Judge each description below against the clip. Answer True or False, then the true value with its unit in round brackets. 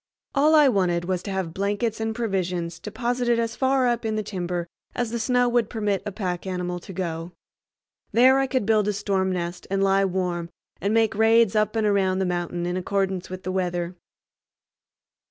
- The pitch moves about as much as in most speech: True (3.9 semitones)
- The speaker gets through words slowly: False (190 wpm)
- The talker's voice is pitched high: True (195 Hz)